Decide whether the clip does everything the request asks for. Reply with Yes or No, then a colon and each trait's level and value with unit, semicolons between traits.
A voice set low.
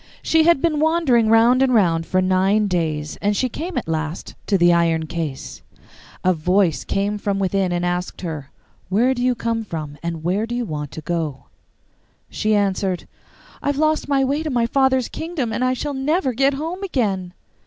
No: high, 210 Hz